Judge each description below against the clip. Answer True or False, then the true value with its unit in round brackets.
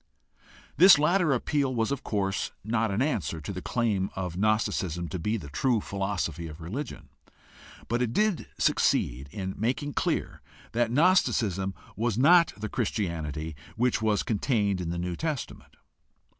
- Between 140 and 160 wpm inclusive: True (150 wpm)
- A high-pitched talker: False (110 Hz)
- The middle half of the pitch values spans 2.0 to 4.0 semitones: False (5.5 semitones)